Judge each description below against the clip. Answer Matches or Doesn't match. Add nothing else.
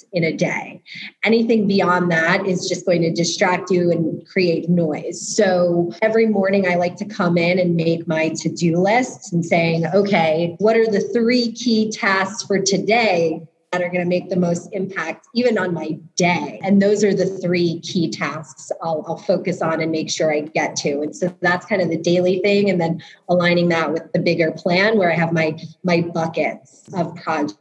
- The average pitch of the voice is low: Doesn't match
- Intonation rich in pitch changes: Doesn't match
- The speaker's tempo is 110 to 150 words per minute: Doesn't match